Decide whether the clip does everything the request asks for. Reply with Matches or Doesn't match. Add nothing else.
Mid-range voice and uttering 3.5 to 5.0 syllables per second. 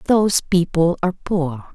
Matches